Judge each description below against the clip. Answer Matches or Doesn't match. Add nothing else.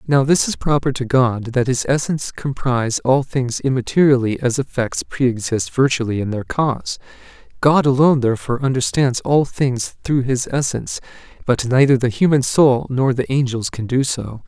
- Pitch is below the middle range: Matches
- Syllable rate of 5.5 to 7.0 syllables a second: Doesn't match